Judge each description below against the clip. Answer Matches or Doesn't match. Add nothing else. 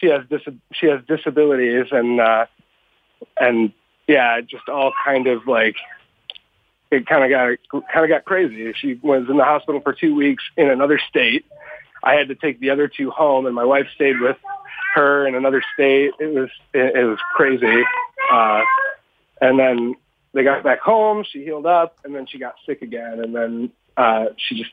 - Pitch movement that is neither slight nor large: Matches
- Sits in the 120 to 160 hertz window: Matches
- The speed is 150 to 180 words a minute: Doesn't match